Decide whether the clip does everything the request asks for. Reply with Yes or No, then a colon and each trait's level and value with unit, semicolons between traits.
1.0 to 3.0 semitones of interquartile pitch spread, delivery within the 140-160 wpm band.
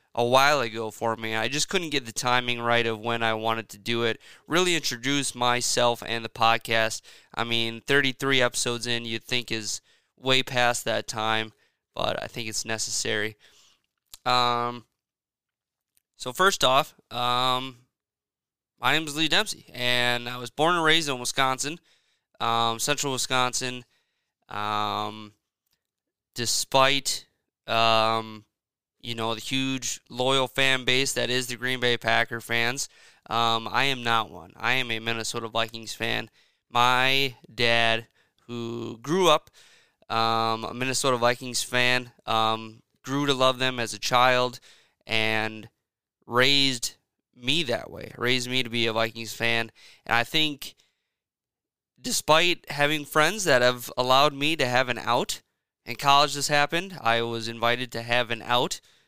Yes: narrow, 2.5 semitones; average, 150 wpm